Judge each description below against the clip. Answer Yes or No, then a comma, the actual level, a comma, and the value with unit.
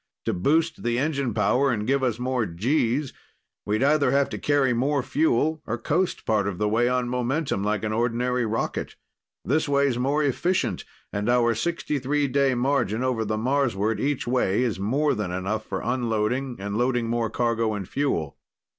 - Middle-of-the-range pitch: No, low, 125 Hz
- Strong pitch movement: No, average, 4.2 semitones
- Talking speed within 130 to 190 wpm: Yes, average, 175 wpm